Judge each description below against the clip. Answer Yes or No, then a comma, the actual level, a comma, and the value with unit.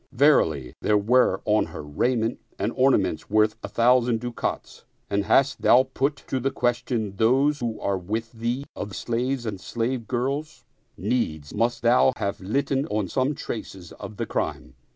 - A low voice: Yes, low, 115 Hz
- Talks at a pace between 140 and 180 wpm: Yes, average, 165 wpm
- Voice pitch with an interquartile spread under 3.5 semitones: No, average, 3.9 semitones